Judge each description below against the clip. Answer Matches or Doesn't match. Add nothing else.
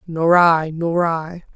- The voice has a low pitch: Doesn't match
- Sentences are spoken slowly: Matches